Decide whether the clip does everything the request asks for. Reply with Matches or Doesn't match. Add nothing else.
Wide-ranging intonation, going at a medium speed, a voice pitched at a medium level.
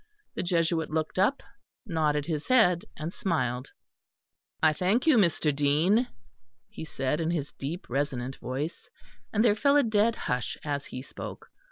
Matches